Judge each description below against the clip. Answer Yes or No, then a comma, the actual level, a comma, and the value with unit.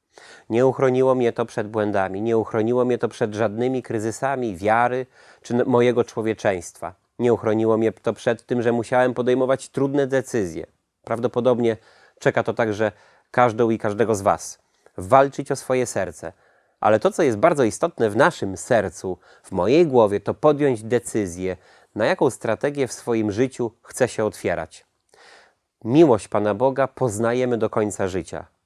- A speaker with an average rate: Yes, average, 150 wpm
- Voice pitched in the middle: No, low, 120 Hz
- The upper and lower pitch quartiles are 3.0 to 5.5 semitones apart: No, narrow, 2.6 semitones